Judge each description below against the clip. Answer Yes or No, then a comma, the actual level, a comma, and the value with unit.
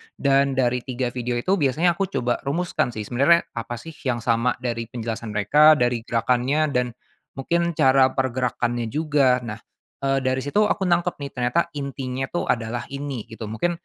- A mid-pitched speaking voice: No, low, 130 Hz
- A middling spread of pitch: Yes, average, 3.3 semitones